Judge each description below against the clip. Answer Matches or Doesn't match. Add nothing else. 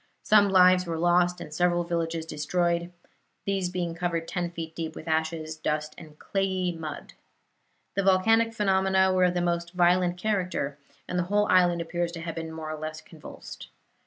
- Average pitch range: Doesn't match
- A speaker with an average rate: Matches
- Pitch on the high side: Doesn't match